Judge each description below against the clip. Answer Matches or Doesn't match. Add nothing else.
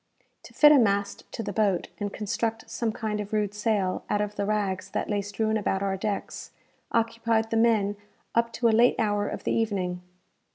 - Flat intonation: Matches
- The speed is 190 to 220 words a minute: Matches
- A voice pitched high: Matches